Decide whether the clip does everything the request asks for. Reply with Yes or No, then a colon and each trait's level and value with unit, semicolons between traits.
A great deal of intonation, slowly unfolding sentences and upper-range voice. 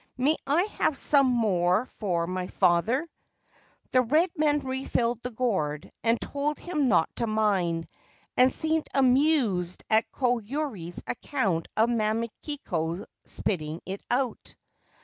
Yes: wide, 7.0 semitones; slow, 130 wpm; high, 235 Hz